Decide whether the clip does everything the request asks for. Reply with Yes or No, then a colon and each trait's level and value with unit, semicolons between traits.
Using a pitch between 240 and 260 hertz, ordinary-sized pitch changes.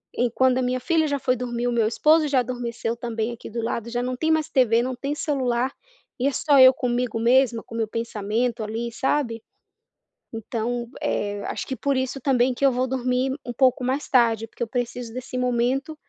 No: high, 245 Hz; narrow, 2.0 semitones